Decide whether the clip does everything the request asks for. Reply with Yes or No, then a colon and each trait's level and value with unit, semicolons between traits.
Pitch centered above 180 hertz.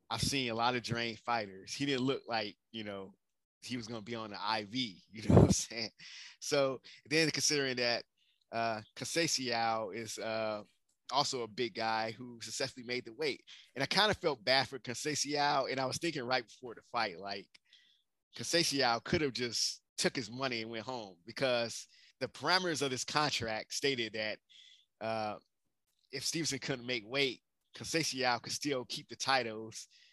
No: low, 125 Hz